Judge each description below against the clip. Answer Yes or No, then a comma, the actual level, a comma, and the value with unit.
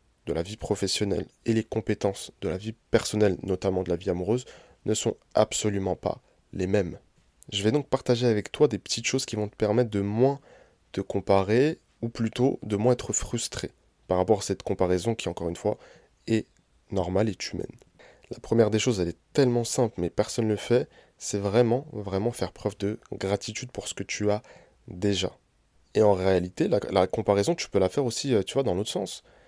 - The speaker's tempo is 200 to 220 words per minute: Yes, average, 205 wpm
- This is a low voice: Yes, low, 105 Hz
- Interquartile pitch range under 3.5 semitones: Yes, average, 3.1 semitones